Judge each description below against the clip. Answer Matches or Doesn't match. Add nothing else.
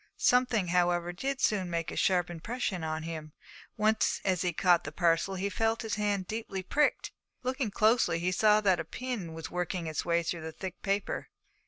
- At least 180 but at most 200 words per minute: Matches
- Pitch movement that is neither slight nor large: Matches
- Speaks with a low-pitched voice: Doesn't match